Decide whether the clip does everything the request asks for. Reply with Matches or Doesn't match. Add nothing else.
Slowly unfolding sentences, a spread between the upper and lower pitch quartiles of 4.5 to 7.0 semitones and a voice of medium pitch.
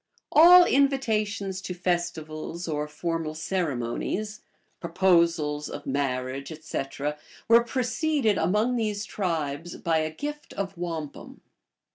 Matches